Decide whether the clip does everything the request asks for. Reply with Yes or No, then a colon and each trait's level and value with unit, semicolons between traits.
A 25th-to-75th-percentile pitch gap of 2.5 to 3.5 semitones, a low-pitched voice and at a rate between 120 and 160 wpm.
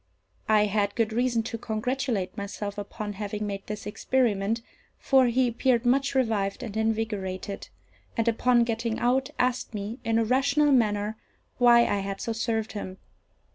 No: average, 2.9 semitones; high, 225 Hz; average, 155 wpm